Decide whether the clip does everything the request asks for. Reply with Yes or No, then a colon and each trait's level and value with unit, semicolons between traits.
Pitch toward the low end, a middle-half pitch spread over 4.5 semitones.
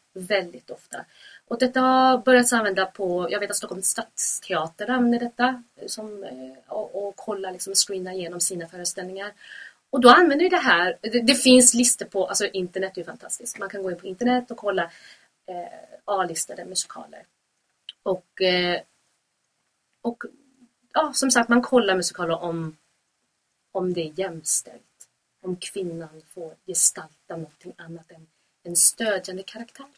No: high, 195 Hz; average, 5.1 semitones